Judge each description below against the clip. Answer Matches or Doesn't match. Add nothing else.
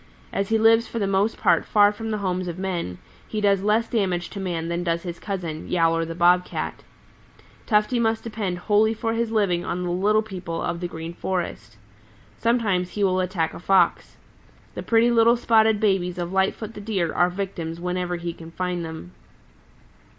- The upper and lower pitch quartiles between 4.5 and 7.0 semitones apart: Doesn't match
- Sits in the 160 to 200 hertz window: Matches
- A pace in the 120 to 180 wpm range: Doesn't match